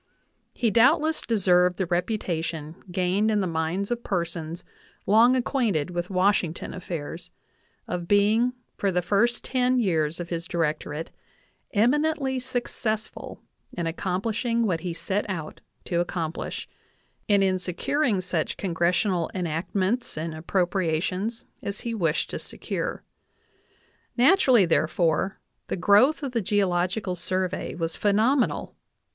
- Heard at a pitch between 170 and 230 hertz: Yes, medium, 185 Hz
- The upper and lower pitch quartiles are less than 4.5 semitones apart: No, average, 4.8 semitones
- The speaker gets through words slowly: Yes, slow, 125 wpm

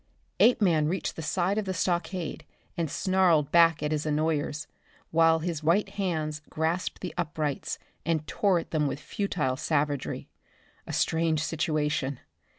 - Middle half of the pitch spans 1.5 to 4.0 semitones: Yes, average, 2.7 semitones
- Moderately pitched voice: Yes, medium, 160 Hz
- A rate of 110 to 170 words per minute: Yes, average, 145 wpm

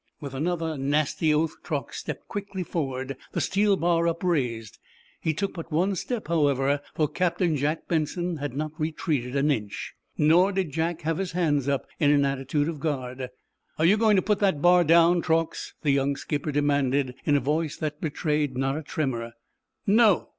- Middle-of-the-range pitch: Yes, medium, 155 Hz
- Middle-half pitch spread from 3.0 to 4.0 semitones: Yes, average, 3.4 semitones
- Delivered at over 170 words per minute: Yes, average, 180 wpm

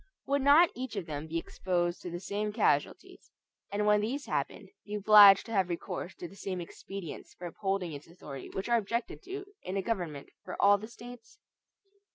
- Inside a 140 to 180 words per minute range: No, average, 195 wpm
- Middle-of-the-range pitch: No, high, 200 Hz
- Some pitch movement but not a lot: Yes, average, 4.6 semitones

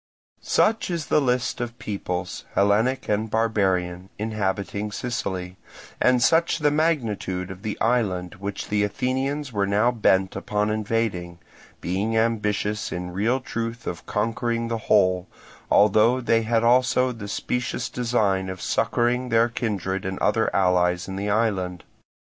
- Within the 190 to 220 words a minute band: No, average, 140 wpm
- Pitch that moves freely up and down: No, average, 3.9 semitones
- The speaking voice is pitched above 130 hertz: No, low, 105 Hz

